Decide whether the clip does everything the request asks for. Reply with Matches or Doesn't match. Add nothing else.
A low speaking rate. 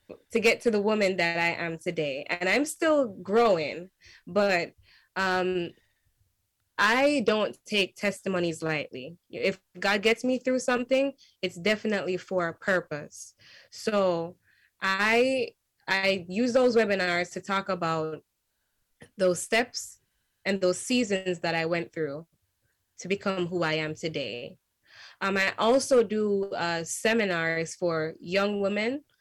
Matches